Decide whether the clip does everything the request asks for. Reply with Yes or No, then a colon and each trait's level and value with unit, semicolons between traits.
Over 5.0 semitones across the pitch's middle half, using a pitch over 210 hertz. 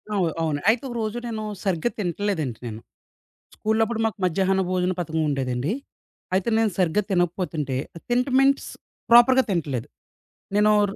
No: wide, 5.5 semitones; high, 190 Hz